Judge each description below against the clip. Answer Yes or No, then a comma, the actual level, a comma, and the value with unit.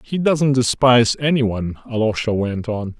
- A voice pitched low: Yes, low, 120 Hz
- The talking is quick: No, average, 160 wpm